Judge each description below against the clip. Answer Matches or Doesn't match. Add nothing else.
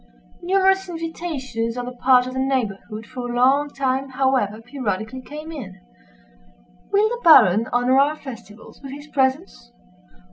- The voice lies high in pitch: Matches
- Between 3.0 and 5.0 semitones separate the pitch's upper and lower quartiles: Matches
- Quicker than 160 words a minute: Doesn't match